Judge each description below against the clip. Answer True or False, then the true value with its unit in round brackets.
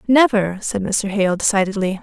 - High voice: True (205 Hz)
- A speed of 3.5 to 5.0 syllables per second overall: True (4.9 syllables/s)